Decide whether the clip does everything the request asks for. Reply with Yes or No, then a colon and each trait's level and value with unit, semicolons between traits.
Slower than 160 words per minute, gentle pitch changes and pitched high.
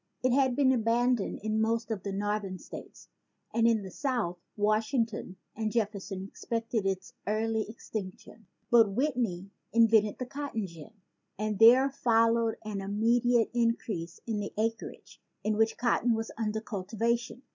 Yes: average, 150 wpm; narrow, 2.2 semitones; high, 225 Hz